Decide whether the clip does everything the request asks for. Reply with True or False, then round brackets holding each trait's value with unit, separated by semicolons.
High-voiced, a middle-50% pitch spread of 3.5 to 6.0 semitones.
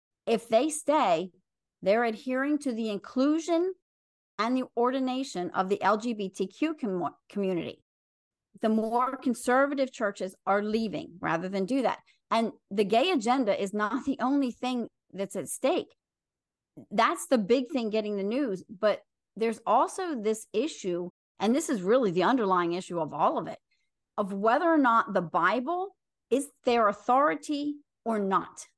True (230 Hz; 5.1 semitones)